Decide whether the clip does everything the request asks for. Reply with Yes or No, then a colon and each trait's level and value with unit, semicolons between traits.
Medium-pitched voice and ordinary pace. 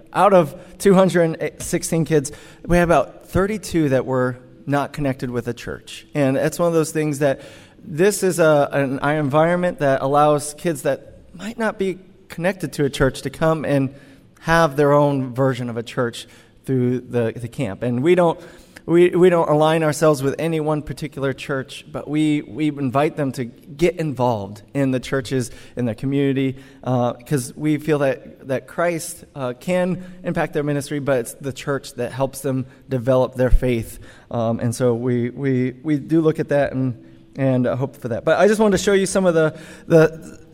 Yes: medium, 145 Hz; average, 190 wpm